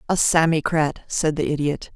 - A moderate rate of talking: Yes, average, 155 wpm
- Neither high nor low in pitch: Yes, medium, 155 Hz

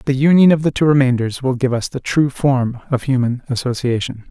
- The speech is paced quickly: Yes, fast, 210 wpm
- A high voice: No, low, 130 Hz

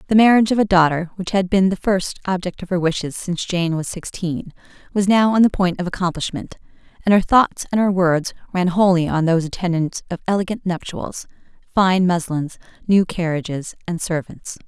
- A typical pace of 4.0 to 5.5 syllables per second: Yes, 5.4 syllables/s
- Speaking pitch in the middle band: Yes, medium, 180 Hz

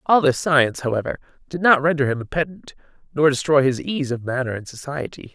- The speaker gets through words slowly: No, average, 200 wpm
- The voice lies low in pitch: No, medium, 145 Hz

